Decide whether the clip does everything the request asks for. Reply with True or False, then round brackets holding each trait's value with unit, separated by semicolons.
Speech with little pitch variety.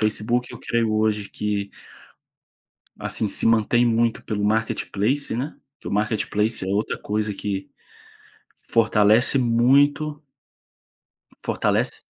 True (2.2 semitones)